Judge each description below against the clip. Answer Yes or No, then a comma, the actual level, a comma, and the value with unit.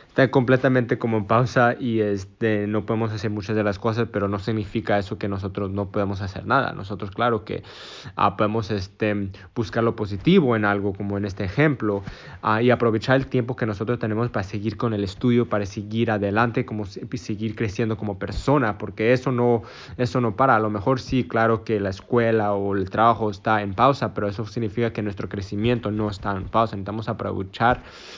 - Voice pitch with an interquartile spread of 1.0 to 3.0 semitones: Yes, narrow, 2.6 semitones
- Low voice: Yes, low, 110 Hz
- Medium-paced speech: No, fast, 200 wpm